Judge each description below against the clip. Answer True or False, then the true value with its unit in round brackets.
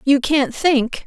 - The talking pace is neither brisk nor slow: True (170 wpm)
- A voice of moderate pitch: False (275 Hz)